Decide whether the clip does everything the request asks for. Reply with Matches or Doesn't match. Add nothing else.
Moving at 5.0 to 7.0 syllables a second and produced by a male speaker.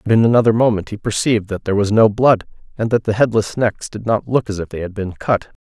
Matches